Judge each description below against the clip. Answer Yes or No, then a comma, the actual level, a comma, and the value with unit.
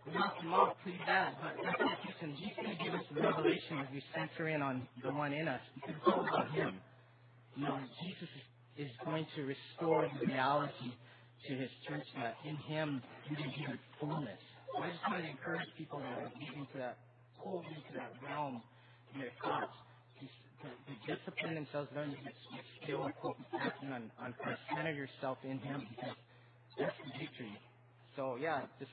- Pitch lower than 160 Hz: Yes, medium, 140 Hz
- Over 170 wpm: Yes, average, 180 wpm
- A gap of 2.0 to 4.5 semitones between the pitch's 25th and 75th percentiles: Yes, average, 3.6 semitones